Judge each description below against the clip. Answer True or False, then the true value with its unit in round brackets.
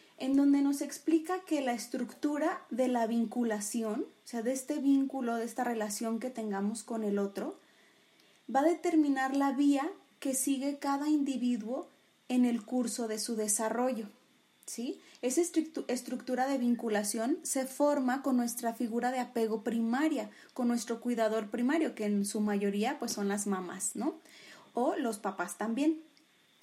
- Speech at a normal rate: True (155 wpm)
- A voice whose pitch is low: False (250 Hz)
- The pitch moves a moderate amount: True (3.8 semitones)